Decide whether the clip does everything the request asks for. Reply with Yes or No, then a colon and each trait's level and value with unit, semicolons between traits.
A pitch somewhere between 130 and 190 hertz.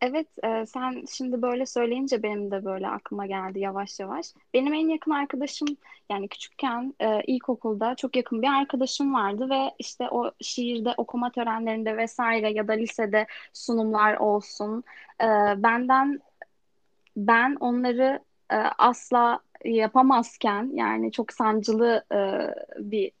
No: high, 235 Hz